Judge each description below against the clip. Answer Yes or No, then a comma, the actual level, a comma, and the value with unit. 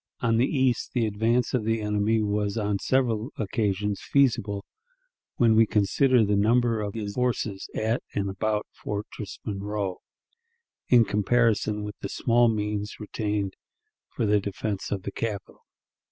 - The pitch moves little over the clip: Yes, narrow, 2.1 semitones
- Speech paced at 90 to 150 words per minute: Yes, average, 145 wpm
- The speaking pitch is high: No, low, 105 Hz